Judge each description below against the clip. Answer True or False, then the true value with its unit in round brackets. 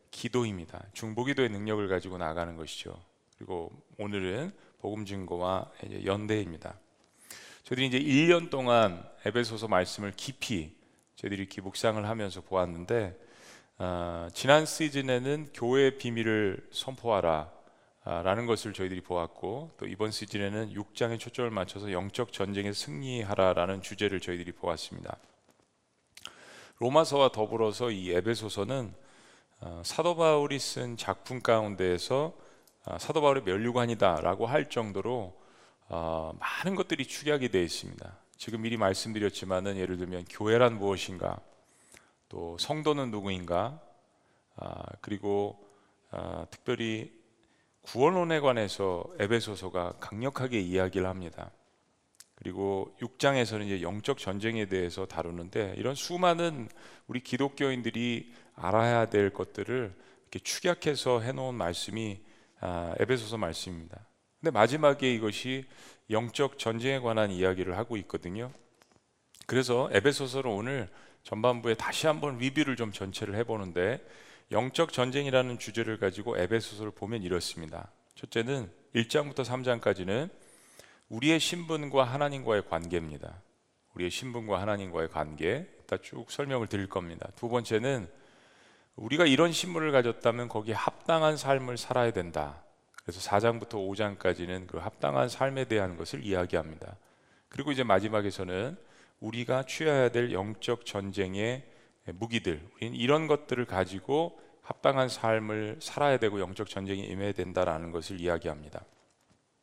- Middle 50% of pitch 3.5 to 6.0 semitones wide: True (5.1 semitones)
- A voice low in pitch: True (110 Hz)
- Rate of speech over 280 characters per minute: True (310 characters per minute)